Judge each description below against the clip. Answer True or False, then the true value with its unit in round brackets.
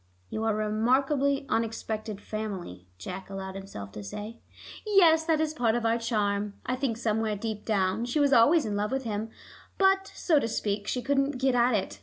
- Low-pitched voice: False (225 Hz)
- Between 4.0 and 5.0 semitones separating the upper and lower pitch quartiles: True (4.6 semitones)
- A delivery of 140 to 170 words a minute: False (195 wpm)